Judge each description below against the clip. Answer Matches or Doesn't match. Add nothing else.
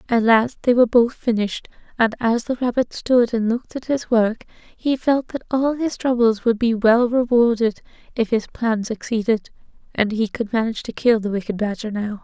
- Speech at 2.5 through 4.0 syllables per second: Doesn't match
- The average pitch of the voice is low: Doesn't match